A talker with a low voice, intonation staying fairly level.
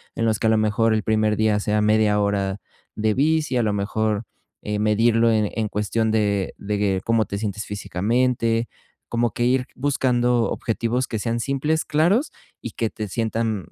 Yes: low, 110 Hz; narrow, 2.2 semitones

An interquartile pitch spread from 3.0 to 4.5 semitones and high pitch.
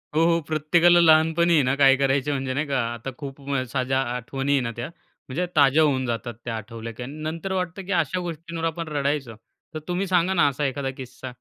No: average, 4.1 semitones; medium, 145 Hz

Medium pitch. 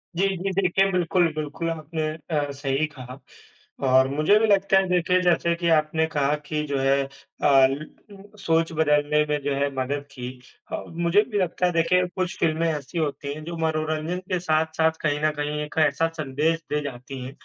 Yes: medium, 155 Hz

